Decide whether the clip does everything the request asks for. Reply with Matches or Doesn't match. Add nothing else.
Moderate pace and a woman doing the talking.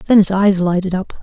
Doesn't match